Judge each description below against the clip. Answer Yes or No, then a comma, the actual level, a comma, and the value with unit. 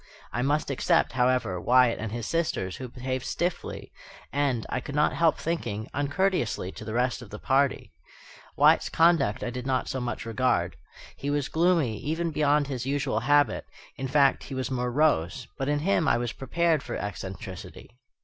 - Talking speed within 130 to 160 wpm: No, average, 175 wpm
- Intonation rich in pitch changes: No, average, 3.7 semitones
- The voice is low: Yes, low, 130 Hz